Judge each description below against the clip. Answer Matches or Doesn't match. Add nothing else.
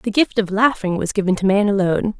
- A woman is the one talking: Matches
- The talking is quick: Matches